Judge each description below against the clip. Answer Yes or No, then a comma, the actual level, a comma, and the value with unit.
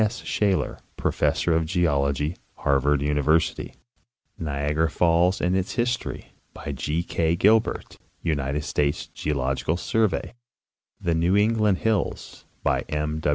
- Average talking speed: No, slow, 120 wpm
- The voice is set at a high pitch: No, very low, 80 Hz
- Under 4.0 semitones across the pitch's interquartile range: No, average, 4.3 semitones